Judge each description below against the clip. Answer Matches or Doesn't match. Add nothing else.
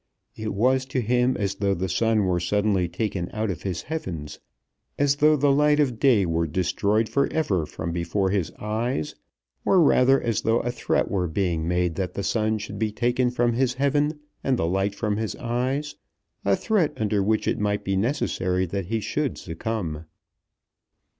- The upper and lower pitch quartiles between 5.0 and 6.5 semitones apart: Matches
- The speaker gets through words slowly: Doesn't match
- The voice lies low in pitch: Matches